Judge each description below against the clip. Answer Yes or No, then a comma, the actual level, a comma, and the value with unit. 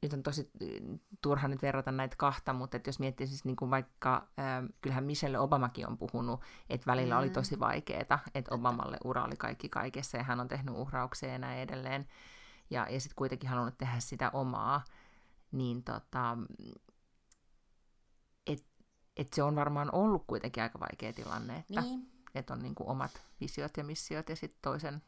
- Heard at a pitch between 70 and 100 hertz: No, low, 130 Hz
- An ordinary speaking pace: No, fast, 170 wpm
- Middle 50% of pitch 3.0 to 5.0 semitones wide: No, narrow, 2.5 semitones